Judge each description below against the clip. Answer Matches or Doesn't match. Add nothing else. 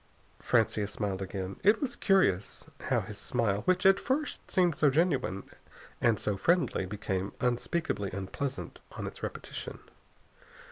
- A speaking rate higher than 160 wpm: Doesn't match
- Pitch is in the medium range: Doesn't match